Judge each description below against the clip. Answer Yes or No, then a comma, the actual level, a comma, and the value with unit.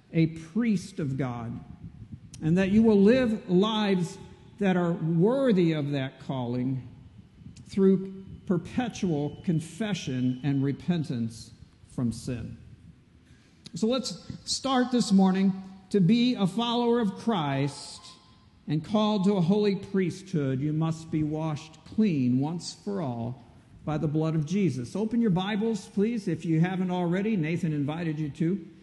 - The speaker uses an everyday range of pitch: No, wide, 5.7 semitones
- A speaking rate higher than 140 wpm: No, slow, 135 wpm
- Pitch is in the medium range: Yes, medium, 170 Hz